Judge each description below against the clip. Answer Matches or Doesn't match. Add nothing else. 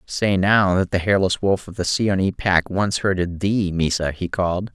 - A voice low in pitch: Matches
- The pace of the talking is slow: Doesn't match